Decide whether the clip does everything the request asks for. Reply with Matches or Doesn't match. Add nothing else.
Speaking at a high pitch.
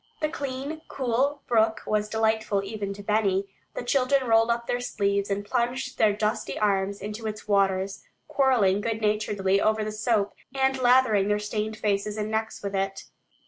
Matches